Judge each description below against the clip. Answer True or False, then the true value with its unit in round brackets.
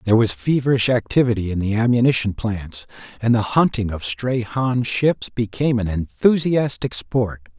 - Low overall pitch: True (115 Hz)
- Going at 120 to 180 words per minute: True (150 wpm)